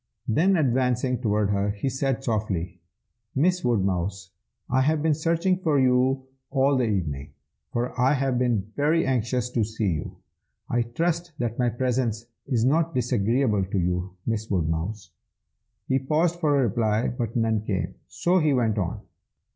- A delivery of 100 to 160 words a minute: Yes, average, 155 wpm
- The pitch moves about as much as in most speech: Yes, average, 4.5 semitones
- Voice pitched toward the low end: Yes, low, 120 Hz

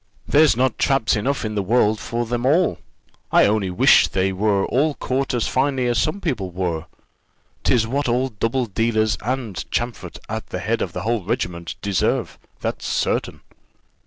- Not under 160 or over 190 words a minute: Yes, average, 170 wpm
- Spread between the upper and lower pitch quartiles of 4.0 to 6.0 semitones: Yes, average, 4.4 semitones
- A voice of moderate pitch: No, low, 115 Hz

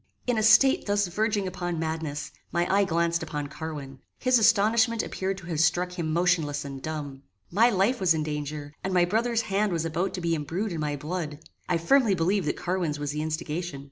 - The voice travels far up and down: No, average, 4.4 semitones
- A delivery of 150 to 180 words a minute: No, fast, 205 wpm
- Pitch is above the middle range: No, medium, 170 Hz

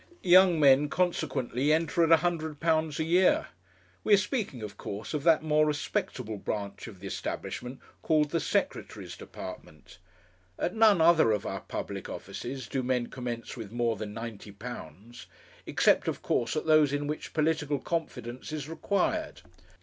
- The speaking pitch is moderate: Yes, medium, 145 Hz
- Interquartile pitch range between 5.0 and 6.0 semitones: Yes, wide, 5.4 semitones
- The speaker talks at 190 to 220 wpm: No, average, 150 wpm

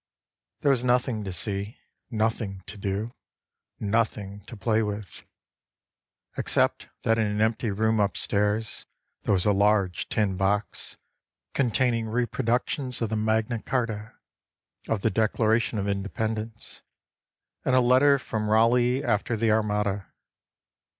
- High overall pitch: No, low, 110 Hz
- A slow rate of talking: Yes, slow, 130 wpm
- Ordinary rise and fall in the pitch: No, narrow, 2.1 semitones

